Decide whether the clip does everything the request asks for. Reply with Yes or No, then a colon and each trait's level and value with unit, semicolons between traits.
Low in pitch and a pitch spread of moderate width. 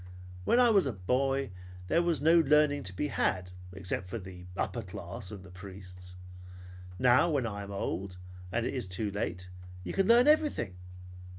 No: low, 105 Hz; wide, 7.8 semitones